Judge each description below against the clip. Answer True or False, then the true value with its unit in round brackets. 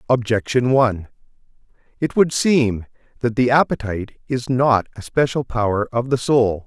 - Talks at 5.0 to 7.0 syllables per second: False (4.7 syllables/s)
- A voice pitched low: True (120 Hz)